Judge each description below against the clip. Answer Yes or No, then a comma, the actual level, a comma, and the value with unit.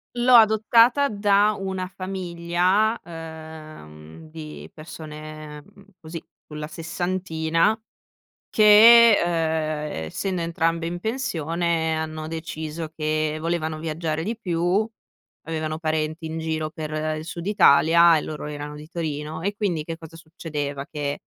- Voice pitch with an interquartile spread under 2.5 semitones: No, average, 2.8 semitones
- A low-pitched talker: No, medium, 165 Hz